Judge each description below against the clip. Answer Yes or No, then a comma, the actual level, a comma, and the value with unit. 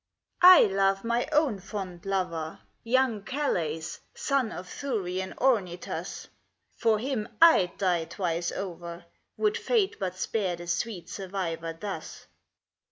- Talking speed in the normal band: No, slow, 125 wpm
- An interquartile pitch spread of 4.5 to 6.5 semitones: Yes, average, 5.0 semitones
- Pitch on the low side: No, high, 195 Hz